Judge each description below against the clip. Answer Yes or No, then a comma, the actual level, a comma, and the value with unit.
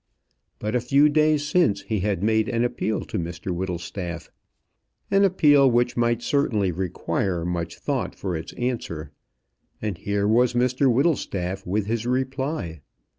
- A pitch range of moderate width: No, wide, 6.5 semitones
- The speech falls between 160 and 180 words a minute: No, average, 145 wpm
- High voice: No, low, 110 Hz